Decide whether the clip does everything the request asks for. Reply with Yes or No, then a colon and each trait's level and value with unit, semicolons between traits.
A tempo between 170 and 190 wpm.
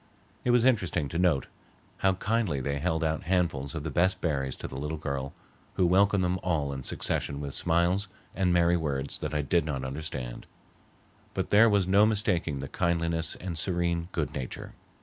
Yes: average, 185 wpm